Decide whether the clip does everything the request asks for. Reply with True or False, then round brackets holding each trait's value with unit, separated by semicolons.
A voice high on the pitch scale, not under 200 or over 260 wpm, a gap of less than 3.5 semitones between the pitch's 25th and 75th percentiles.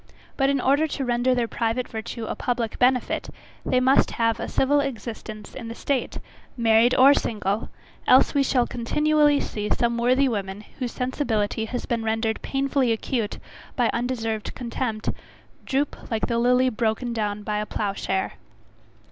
False (240 Hz; 160 wpm; 2.7 semitones)